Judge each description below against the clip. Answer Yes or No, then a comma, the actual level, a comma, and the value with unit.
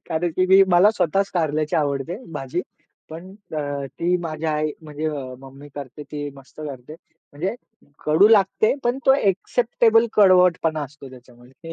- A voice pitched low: No, medium, 155 Hz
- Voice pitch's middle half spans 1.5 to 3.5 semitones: No, average, 4.7 semitones